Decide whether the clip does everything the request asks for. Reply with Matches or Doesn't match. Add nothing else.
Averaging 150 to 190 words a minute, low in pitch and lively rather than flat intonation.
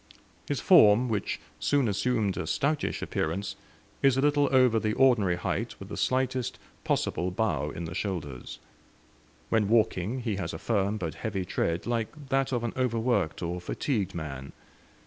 Matches